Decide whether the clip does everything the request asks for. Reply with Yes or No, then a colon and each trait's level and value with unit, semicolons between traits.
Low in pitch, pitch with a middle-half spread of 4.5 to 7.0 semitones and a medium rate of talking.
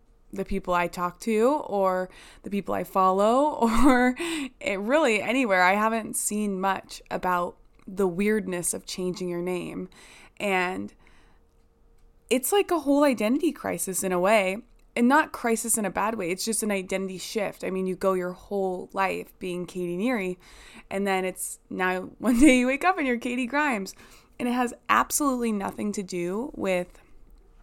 No: high, 200 Hz; average, 5.2 semitones; average, 170 wpm